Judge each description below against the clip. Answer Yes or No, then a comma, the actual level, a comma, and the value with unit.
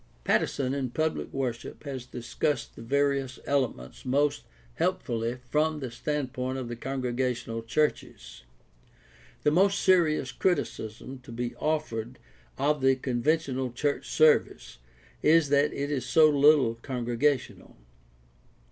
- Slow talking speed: Yes, slow, 120 wpm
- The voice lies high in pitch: No, low, 135 Hz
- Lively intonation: No, average, 3.5 semitones